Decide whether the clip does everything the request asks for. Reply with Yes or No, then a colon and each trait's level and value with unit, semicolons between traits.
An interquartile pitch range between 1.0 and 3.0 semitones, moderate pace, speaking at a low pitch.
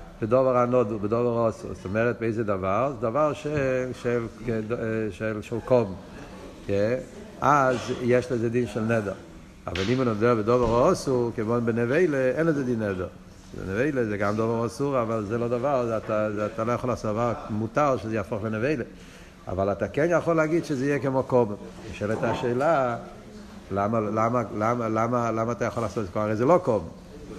No: narrow, 2.5 semitones; fast, 170 wpm; low, 115 Hz